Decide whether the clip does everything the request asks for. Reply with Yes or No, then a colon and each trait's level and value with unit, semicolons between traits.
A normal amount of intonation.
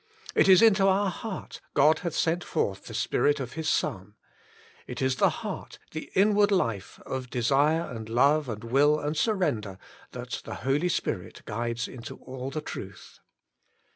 No: wide, 6.2 semitones